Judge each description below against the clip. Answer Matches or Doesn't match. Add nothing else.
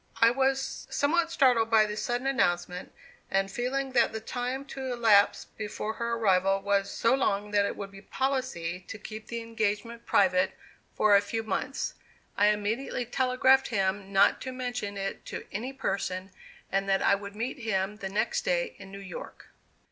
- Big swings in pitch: Doesn't match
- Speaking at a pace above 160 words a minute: Matches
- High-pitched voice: Matches